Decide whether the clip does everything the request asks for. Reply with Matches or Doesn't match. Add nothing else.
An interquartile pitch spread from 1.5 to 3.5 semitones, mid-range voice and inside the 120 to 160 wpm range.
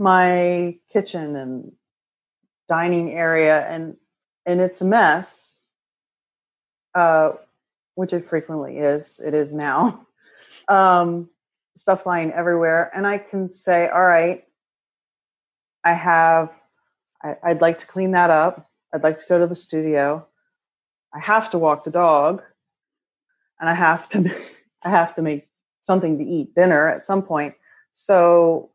Matches